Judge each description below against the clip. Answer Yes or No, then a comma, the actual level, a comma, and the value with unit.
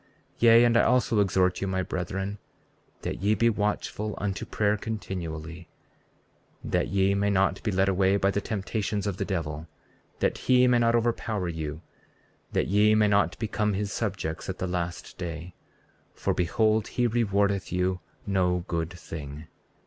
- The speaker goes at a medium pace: Yes, average, 165 wpm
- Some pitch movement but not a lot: Yes, average, 3.0 semitones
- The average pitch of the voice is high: No, low, 100 Hz